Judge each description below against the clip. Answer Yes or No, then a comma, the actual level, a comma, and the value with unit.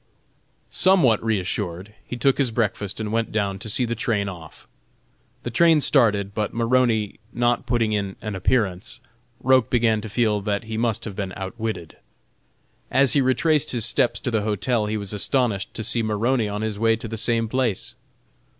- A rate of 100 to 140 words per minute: No, average, 175 wpm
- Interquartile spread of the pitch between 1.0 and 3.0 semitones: Yes, average, 2.7 semitones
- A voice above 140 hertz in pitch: No, low, 110 Hz